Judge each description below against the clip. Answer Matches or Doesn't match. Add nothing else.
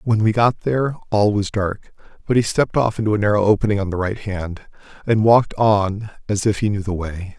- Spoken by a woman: Doesn't match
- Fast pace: Matches